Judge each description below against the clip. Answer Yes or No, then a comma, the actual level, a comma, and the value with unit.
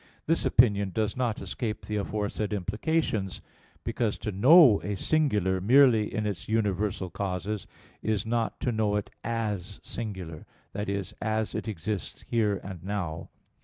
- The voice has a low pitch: Yes, low, 105 Hz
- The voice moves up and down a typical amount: No, narrow, 2.3 semitones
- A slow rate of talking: No, average, 145 wpm